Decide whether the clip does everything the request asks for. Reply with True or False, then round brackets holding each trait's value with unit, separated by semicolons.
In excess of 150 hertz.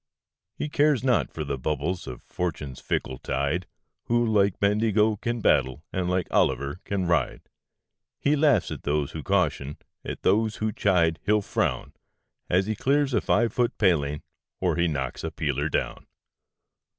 False (95 Hz)